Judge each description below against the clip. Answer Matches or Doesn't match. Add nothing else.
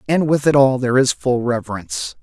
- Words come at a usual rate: Doesn't match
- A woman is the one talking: Doesn't match